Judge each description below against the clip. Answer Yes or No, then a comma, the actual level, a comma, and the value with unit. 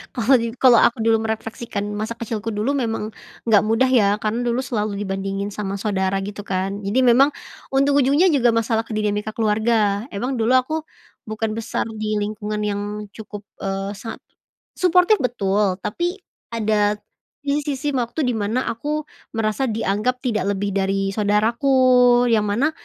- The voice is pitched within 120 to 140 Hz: No, high, 220 Hz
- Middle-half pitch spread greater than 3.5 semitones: No, average, 3.2 semitones